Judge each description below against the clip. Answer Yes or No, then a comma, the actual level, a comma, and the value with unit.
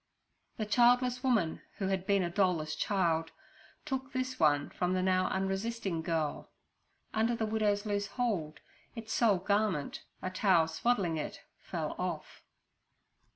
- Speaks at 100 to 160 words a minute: Yes, average, 145 wpm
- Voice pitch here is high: Yes, high, 195 Hz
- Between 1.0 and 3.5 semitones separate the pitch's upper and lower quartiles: No, average, 4.7 semitones